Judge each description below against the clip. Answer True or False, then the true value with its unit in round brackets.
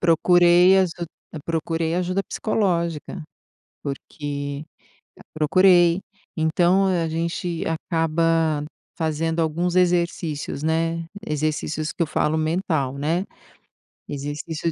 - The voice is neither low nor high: True (165 Hz)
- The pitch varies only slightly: True (2.0 semitones)